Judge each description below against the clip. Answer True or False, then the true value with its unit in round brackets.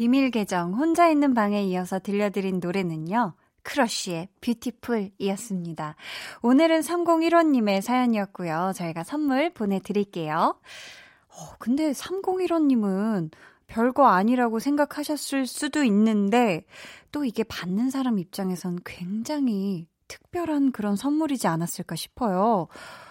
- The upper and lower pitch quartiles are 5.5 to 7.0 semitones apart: True (6.7 semitones)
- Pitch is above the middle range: True (225 Hz)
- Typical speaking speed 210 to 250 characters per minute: False (280 characters per minute)